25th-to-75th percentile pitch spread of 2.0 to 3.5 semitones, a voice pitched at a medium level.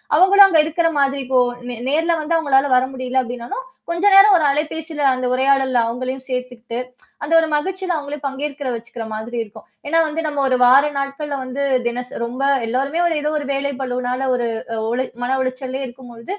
No: average, 3.2 semitones; very high, 270 Hz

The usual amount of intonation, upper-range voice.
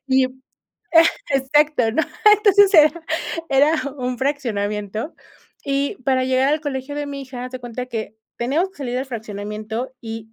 Yes: average, 3.9 semitones; very high, 260 Hz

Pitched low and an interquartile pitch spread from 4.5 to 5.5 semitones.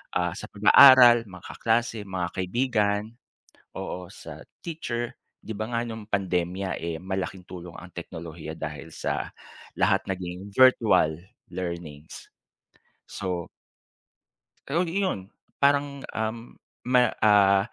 Yes: low, 100 Hz; average, 5.0 semitones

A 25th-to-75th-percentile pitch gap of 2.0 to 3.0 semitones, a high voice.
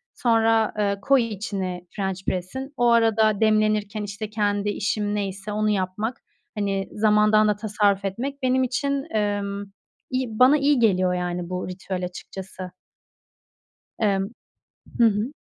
Yes: narrow, 2.5 semitones; high, 210 Hz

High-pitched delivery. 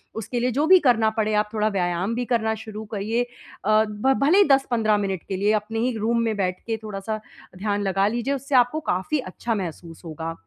Yes: high, 220 Hz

